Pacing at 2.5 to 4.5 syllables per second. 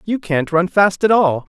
Yes: 4.3 syllables/s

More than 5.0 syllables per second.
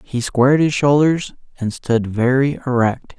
No: 4.2 syllables/s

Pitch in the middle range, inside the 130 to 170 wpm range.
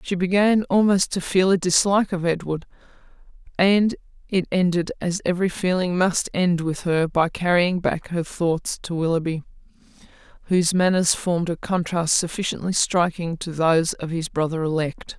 Yes: medium, 175 Hz; average, 155 wpm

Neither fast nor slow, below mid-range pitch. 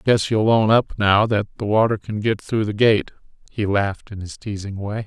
No: fast, 235 wpm; low, 105 Hz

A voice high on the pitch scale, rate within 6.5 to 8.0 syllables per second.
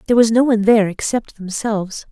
Yes: high, 215 Hz; 6.7 syllables/s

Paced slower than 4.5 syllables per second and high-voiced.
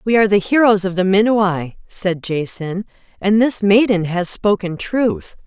Yes: 4.3 syllables/s; high, 200 Hz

